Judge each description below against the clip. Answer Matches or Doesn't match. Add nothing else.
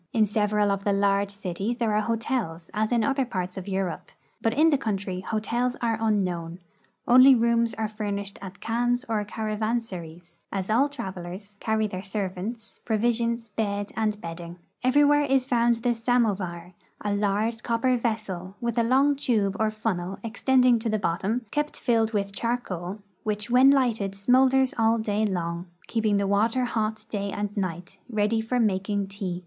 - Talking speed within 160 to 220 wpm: Matches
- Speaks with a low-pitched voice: Doesn't match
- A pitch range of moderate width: Matches